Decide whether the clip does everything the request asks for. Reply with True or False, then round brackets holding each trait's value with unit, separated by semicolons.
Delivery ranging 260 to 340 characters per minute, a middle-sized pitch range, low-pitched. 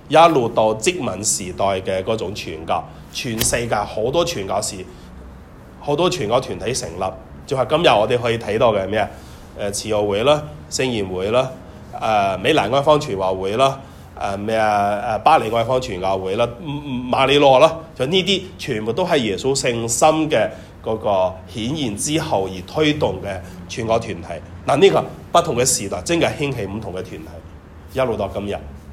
False (265 characters per minute; 6.2 semitones; 110 Hz)